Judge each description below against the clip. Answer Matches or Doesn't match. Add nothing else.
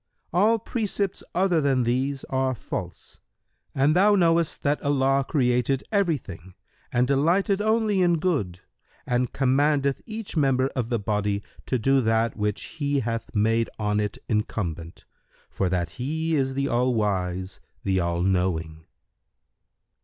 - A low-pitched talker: Matches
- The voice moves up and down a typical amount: Doesn't match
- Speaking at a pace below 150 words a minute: Matches